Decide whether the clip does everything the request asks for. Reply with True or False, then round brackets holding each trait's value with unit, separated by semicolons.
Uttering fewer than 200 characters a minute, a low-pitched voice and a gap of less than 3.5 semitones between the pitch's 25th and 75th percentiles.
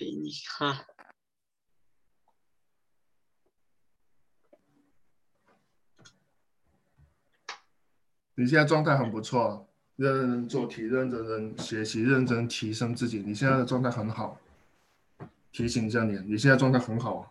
True (165 characters per minute; 120 Hz; 2.7 semitones)